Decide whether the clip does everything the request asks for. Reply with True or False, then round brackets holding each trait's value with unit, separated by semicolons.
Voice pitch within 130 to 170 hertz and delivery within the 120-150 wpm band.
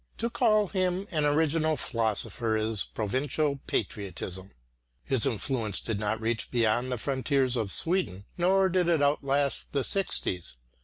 True (135 Hz; 140 wpm)